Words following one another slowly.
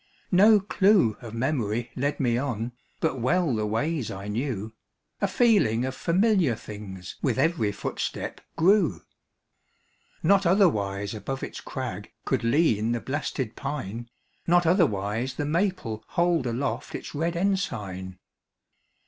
Yes: slow, 130 wpm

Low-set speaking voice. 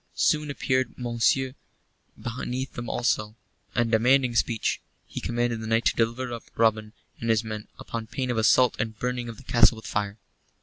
Yes: low, 120 Hz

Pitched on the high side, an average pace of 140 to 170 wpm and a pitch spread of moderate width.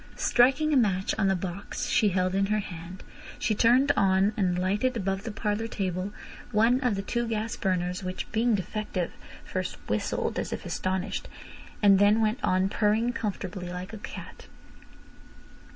Yes: high, 200 Hz; average, 165 wpm; average, 3.2 semitones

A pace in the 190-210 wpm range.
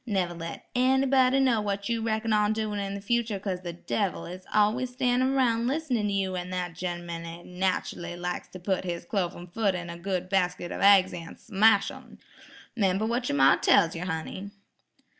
Yes: average, 195 wpm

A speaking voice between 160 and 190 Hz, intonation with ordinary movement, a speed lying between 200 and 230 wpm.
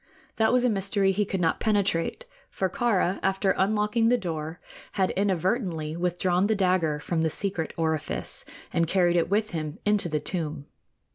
No: medium, 185 Hz; average, 3.7 semitones; average, 165 wpm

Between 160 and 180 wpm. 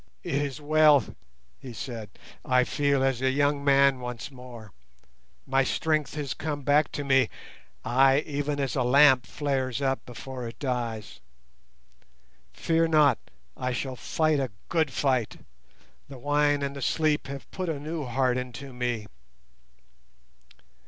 No: average, 145 wpm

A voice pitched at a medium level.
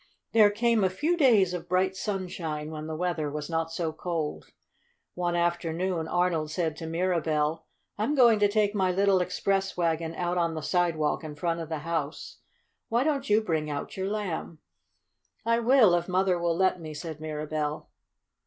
Yes: medium, 175 Hz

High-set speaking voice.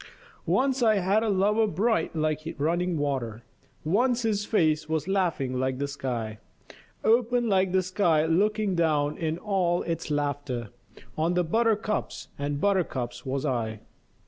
No: medium, 165 Hz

